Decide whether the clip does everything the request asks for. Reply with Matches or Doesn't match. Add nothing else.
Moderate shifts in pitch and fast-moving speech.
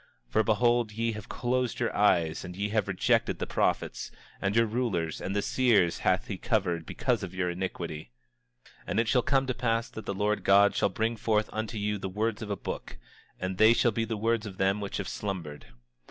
Matches